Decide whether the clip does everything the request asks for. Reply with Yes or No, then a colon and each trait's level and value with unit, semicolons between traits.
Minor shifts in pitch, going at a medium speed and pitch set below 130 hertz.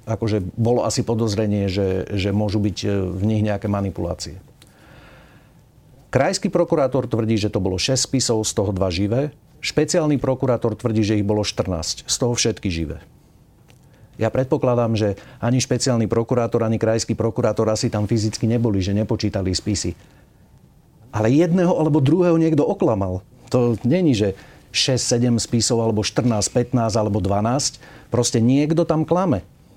No: average, 3.6 semitones; average, 145 wpm; low, 115 Hz